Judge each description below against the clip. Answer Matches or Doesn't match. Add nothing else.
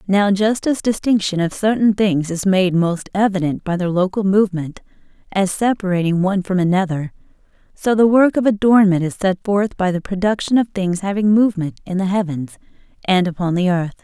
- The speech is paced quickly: Doesn't match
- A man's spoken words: Doesn't match